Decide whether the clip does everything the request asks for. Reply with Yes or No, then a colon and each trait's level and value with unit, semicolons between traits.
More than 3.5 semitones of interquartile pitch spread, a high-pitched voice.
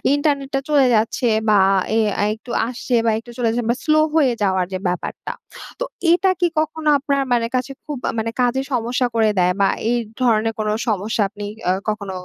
Yes: average, 4.4 semitones; high, 240 Hz